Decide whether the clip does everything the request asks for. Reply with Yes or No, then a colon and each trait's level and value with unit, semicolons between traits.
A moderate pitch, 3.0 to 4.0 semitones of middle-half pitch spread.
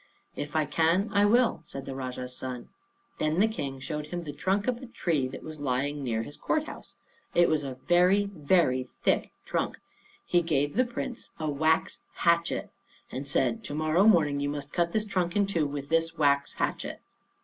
No: medium, 155 Hz; average, 4.6 semitones